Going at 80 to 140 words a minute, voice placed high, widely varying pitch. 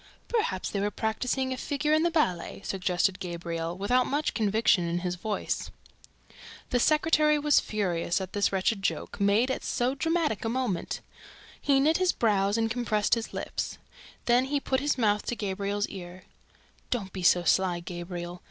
No: average, 170 wpm; high, 210 Hz; wide, 5.9 semitones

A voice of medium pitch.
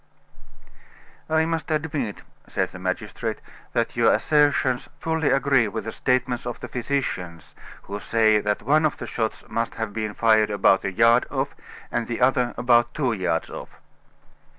No: low, 120 Hz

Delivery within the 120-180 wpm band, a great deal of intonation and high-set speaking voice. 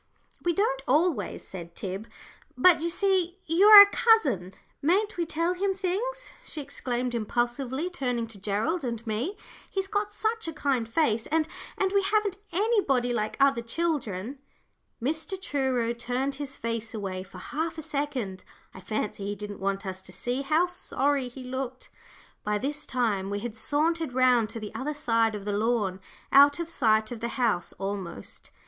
Yes: average, 170 wpm; wide, 7.1 semitones; very high, 260 Hz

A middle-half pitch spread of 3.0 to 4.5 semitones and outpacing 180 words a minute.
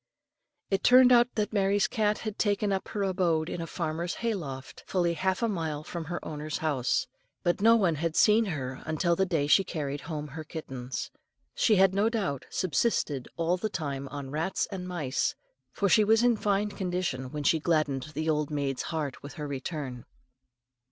No: average, 5.1 semitones; average, 190 wpm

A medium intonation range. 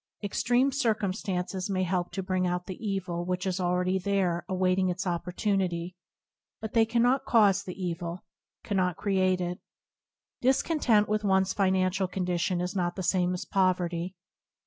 No: narrow, 2.0 semitones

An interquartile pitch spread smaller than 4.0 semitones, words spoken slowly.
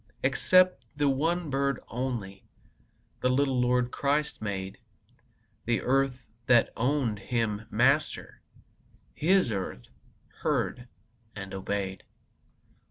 No: average, 4.7 semitones; slow, 100 wpm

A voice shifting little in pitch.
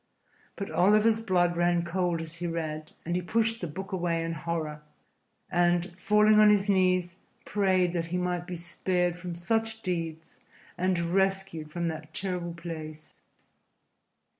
Yes: narrow, 2.3 semitones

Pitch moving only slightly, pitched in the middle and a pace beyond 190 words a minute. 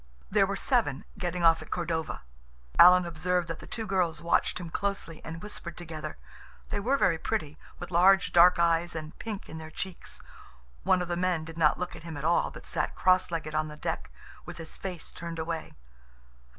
Yes: narrow, 2.0 semitones; medium, 170 Hz; average, 200 wpm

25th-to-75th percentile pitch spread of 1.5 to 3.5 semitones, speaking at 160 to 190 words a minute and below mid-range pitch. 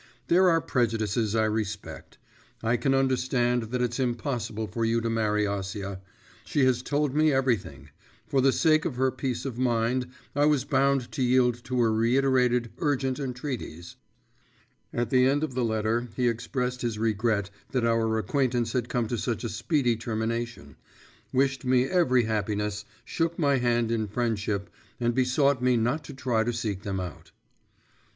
Yes: average, 2.7 semitones; average, 165 wpm; low, 120 Hz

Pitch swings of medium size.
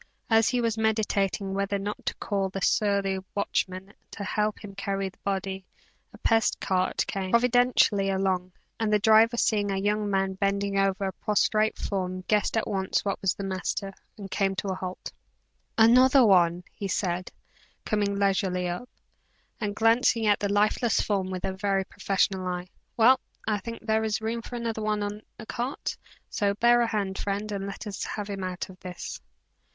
No: narrow, 2.2 semitones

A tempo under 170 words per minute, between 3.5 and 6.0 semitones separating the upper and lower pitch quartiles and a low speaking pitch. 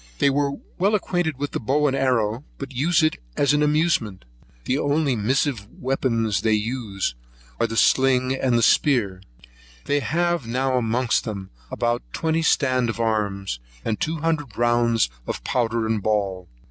Yes: average, 160 wpm; average, 4.5 semitones; low, 125 Hz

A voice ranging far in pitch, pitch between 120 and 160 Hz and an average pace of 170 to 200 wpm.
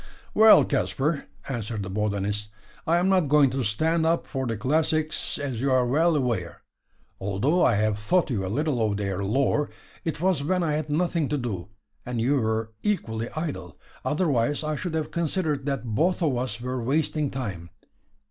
Yes: wide, 6.0 semitones; low, 135 Hz; average, 180 wpm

